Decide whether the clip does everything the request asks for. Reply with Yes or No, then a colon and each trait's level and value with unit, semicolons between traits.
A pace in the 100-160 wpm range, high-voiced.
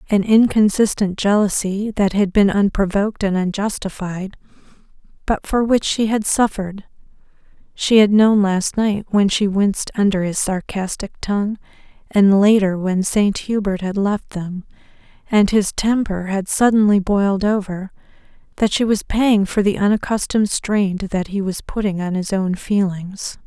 Yes: average, 150 wpm; high, 200 Hz